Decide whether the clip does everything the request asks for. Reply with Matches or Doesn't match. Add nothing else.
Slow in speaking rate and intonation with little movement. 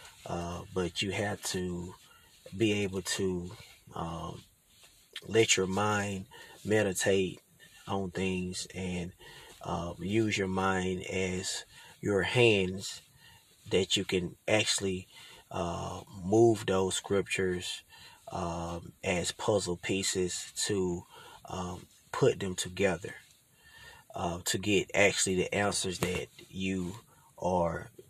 Matches